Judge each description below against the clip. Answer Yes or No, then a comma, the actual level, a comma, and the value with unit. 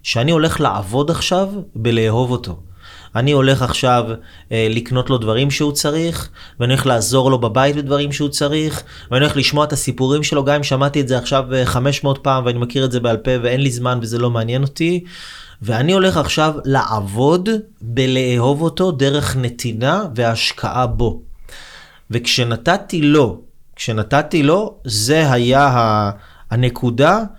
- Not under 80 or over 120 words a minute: No, average, 145 wpm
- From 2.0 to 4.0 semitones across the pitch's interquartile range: Yes, average, 3.6 semitones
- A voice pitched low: Yes, low, 130 Hz